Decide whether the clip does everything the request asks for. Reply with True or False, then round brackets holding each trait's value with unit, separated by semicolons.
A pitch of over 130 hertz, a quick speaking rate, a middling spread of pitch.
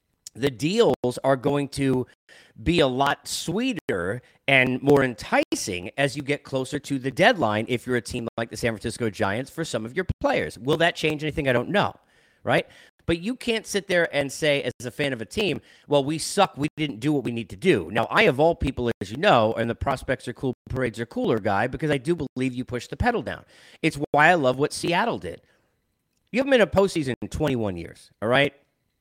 True (140 Hz; 225 wpm; 3.9 semitones)